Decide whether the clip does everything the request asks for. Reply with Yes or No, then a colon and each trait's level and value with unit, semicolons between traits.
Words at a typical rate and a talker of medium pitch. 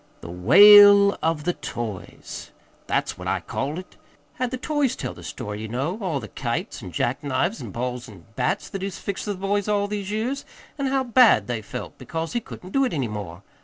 No: fast, 215 wpm; medium, 180 Hz